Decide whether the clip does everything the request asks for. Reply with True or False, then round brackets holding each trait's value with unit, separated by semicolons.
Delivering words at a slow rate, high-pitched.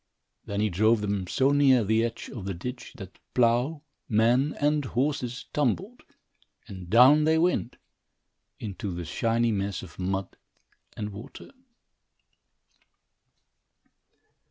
False (120 wpm; 115 Hz)